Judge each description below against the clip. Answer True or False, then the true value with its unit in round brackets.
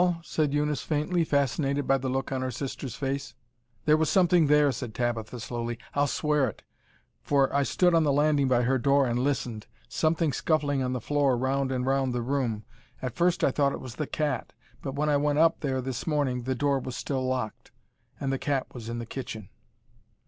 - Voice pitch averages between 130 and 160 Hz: True (135 Hz)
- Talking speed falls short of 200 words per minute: False (205 wpm)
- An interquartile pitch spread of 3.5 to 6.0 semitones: False (2.6 semitones)